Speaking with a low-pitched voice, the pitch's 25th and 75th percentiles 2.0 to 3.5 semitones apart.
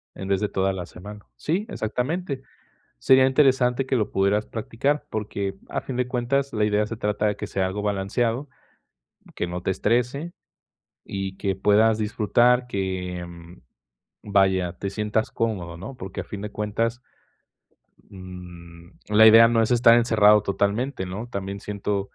No: low, 105 Hz; average, 3.9 semitones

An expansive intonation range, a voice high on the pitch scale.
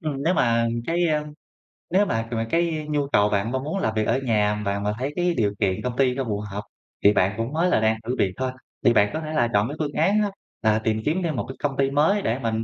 No: wide, 6.0 semitones; low, 125 Hz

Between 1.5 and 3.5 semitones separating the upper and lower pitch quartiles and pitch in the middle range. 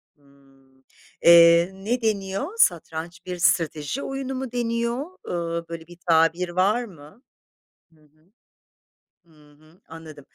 No: average, 4.8 semitones; medium, 170 Hz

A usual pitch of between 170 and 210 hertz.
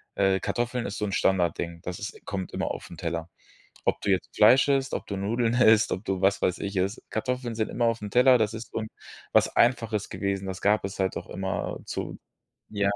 No: low, 100 Hz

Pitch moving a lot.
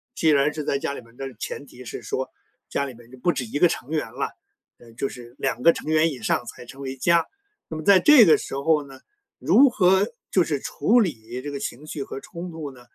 No: average, 4.2 semitones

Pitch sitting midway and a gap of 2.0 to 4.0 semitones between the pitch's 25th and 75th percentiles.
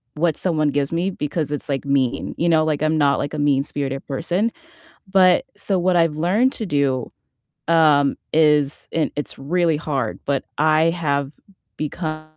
Yes: medium, 155 Hz; average, 2.9 semitones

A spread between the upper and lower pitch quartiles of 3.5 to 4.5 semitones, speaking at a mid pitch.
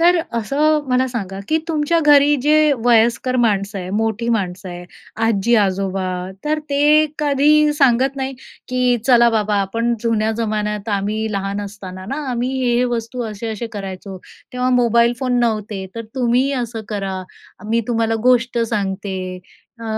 No: average, 3.9 semitones; high, 230 Hz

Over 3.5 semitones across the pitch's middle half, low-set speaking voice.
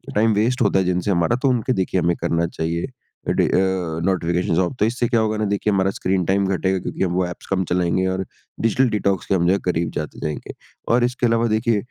Yes: average, 3.9 semitones; very low, 95 Hz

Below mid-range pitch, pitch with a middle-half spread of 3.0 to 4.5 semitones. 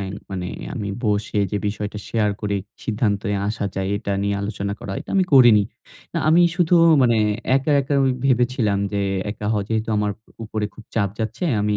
No: low, 105 Hz; narrow, 2.5 semitones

